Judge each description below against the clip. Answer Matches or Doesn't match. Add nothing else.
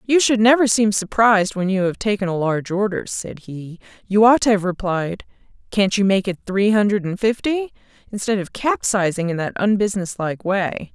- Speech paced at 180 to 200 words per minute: Matches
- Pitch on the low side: Doesn't match